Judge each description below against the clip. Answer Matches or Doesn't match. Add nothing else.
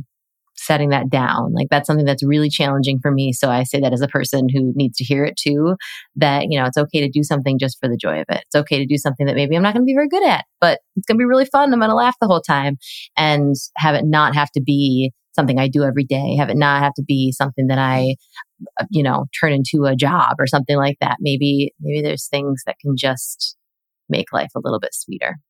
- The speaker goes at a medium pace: Doesn't match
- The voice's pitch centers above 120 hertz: Matches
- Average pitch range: Doesn't match